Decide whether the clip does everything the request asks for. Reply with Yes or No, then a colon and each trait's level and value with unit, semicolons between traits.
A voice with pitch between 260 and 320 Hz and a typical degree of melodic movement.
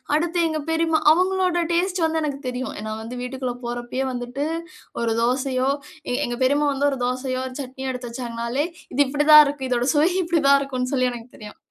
Yes: very high, 265 Hz; average, 3.5 semitones